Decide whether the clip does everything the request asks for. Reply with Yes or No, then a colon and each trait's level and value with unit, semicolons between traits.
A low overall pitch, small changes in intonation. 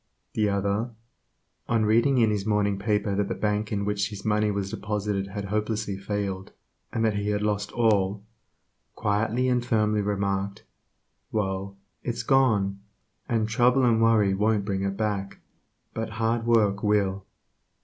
Yes: low, 105 Hz; narrow, 1.9 semitones